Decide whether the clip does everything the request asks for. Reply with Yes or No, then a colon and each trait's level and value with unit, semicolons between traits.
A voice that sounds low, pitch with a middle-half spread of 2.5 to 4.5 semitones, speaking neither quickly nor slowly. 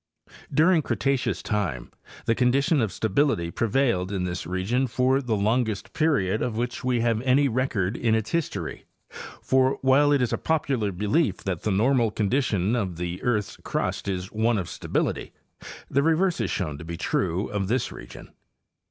No: low, 115 Hz; wide, 5.5 semitones; average, 170 wpm